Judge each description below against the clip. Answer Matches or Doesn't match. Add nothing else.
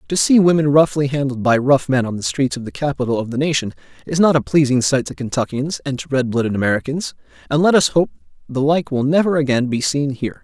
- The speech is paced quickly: Matches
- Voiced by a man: Matches